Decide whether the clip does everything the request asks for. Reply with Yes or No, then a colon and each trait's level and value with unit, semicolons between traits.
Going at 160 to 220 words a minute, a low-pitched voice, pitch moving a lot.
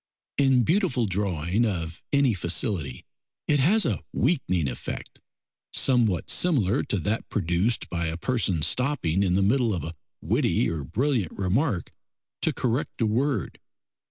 No: average, 140 wpm; low, 105 Hz; wide, 6.8 semitones